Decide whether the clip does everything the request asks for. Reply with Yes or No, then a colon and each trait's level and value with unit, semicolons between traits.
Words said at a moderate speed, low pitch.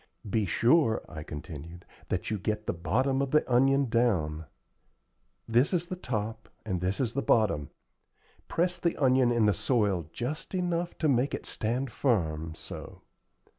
Yes: average, 160 wpm; low, 115 Hz